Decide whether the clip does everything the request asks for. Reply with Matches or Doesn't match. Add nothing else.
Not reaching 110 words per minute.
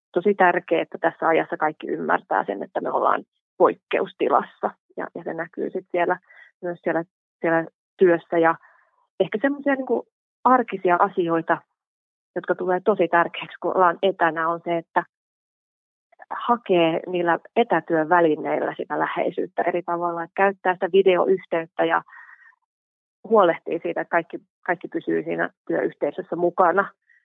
Doesn't match